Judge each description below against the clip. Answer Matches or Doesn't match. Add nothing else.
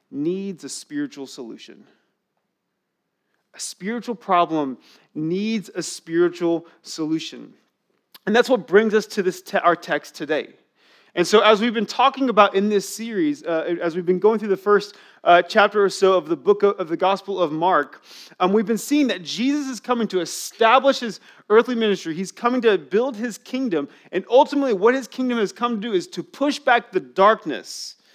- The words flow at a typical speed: Matches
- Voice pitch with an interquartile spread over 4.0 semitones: Matches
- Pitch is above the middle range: Matches